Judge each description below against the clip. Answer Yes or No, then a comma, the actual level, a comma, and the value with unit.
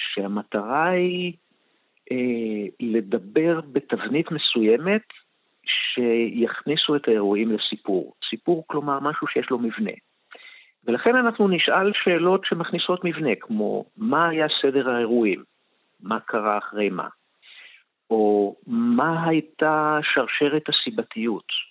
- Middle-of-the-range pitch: Yes, medium, 155 Hz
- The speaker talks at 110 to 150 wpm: No, slow, 100 wpm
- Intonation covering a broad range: Yes, wide, 7.5 semitones